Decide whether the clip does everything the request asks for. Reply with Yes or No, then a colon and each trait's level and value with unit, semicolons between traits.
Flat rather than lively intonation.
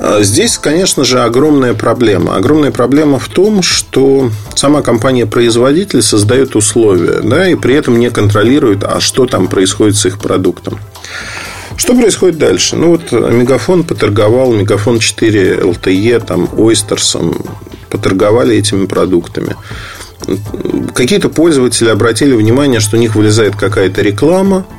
No: average, 4.2 semitones